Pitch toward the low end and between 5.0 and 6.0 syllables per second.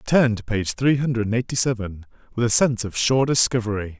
No: low, 115 Hz; 6.3 syllables/s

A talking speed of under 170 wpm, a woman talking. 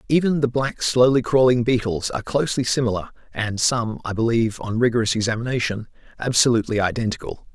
No: average, 145 wpm; male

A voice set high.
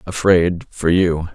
No: very low, 90 Hz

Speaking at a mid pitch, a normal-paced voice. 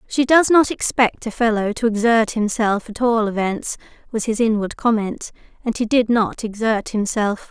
No: high, 225 Hz; average, 175 wpm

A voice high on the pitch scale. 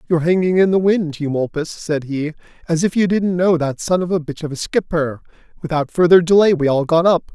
No: medium, 165 Hz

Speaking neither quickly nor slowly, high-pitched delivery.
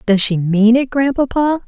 Yes: average, 180 wpm; high, 240 Hz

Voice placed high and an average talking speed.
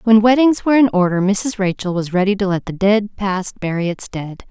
No: high, 200 Hz; fast, 225 wpm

